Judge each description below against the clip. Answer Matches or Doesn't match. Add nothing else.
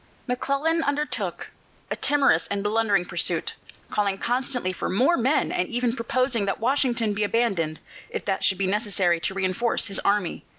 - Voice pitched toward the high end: Matches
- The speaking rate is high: Doesn't match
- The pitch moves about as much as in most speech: Matches